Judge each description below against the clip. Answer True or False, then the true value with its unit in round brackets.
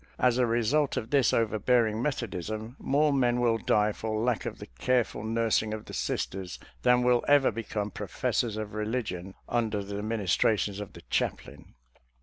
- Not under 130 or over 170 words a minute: True (160 wpm)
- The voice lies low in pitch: True (110 Hz)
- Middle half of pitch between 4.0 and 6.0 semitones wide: False (2.6 semitones)